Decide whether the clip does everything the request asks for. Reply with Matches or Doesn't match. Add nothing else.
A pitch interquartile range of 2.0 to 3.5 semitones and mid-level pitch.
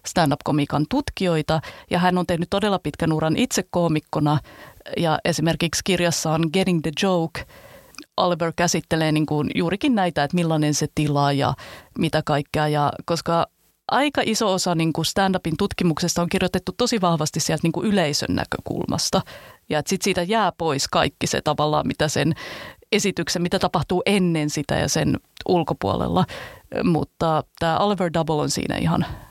Matches